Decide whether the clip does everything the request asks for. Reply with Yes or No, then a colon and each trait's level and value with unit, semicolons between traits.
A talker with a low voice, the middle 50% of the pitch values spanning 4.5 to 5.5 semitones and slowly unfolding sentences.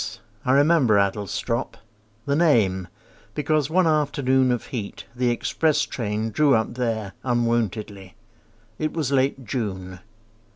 Yes: low, 120 Hz; average, 5.2 semitones; slow, 120 wpm